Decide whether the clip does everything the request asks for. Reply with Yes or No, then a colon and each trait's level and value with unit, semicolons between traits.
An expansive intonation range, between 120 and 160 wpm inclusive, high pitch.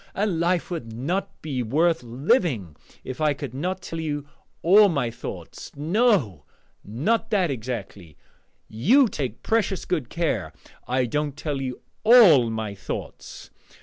No: wide, 7.2 semitones; average, 140 wpm; medium, 150 Hz